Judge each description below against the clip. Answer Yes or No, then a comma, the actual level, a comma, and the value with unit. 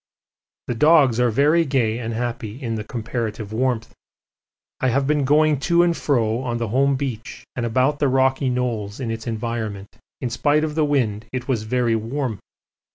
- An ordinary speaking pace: Yes, average, 180 wpm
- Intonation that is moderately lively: Yes, average, 3.6 semitones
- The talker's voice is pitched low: Yes, low, 125 Hz